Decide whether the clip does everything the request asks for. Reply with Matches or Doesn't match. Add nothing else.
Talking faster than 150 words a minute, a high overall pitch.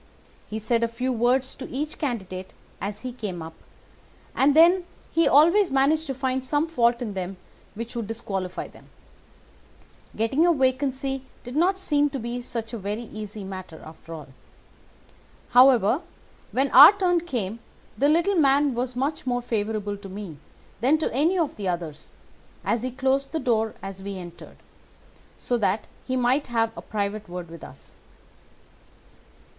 Matches